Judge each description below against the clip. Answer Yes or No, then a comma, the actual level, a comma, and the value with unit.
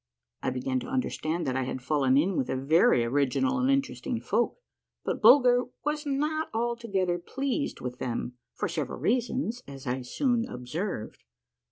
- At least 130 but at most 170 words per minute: Yes, average, 160 wpm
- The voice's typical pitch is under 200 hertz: Yes, medium, 185 Hz